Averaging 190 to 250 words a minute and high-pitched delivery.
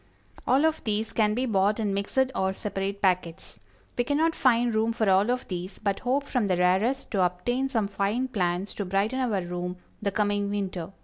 Yes: average, 195 wpm; high, 205 Hz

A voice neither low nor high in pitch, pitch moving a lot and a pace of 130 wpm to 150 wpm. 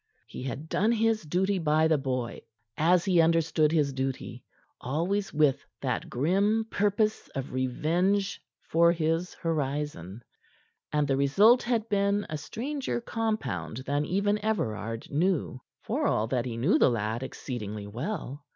Yes: medium, 155 Hz; wide, 7.2 semitones; average, 140 wpm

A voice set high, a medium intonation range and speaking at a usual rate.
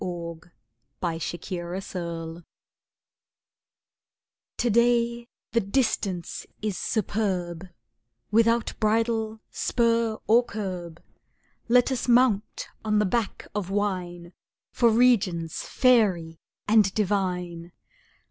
No: high, 205 Hz; average, 4.7 semitones; slow, 90 wpm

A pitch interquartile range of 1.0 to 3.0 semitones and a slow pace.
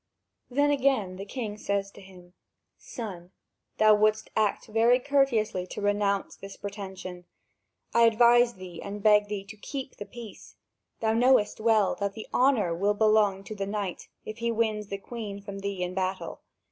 No: narrow, 2.5 semitones; average, 170 wpm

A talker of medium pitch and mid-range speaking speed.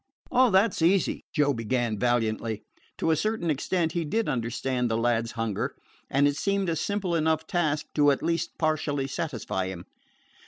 Yes: medium, 145 Hz; average, 170 wpm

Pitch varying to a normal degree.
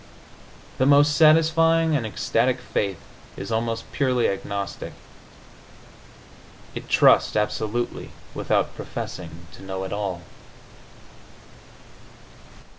No: wide, 6.5 semitones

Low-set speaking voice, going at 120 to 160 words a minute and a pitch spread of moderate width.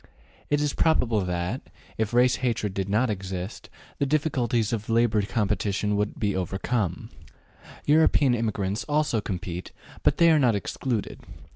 Yes: low, 110 Hz; average, 140 wpm; average, 4.3 semitones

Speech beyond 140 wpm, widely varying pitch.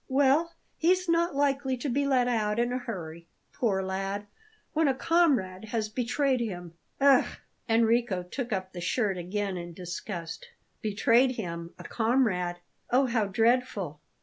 Yes: average, 150 wpm; wide, 5.8 semitones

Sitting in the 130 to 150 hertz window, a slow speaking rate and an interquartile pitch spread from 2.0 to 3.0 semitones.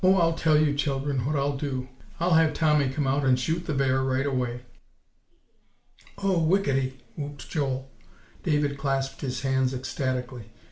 No: medium, 140 Hz; average, 150 wpm; narrow, 2.6 semitones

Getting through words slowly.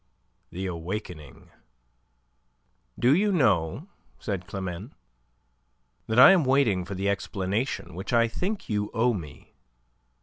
Yes: slow, 115 wpm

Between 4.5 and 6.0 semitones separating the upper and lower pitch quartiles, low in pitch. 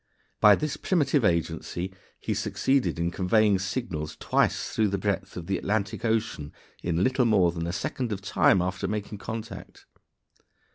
No: average, 3.9 semitones; low, 100 Hz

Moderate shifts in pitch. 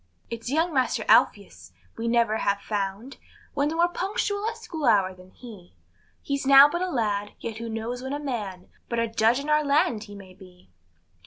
No: wide, 5.9 semitones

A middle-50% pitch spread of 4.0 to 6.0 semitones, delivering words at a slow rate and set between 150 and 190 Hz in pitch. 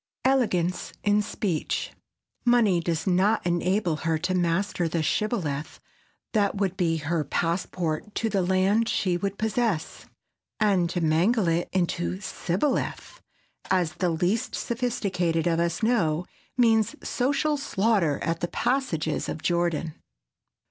Yes: average, 4.4 semitones; slow, 125 wpm; medium, 185 Hz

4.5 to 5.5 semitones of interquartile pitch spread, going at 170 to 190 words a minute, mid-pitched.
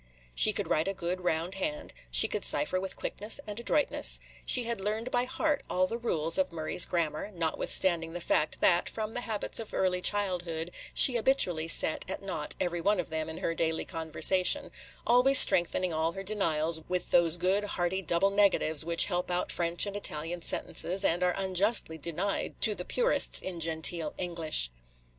No: average, 3.7 semitones; average, 185 wpm; medium, 180 Hz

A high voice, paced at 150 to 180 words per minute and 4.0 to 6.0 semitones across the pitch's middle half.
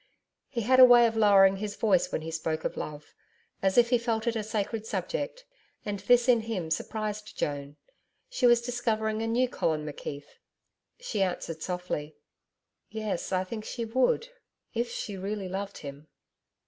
Yes: high, 215 Hz; average, 170 wpm; average, 4.5 semitones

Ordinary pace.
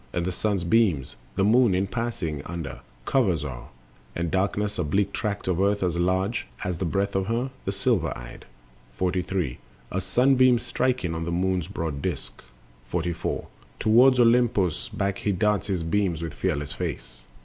Yes: average, 170 wpm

